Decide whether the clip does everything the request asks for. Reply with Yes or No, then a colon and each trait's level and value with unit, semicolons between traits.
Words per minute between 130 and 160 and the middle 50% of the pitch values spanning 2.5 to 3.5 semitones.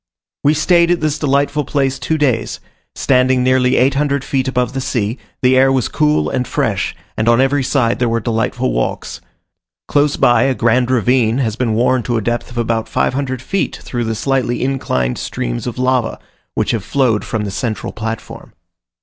No: average, 185 wpm; average, 2.8 semitones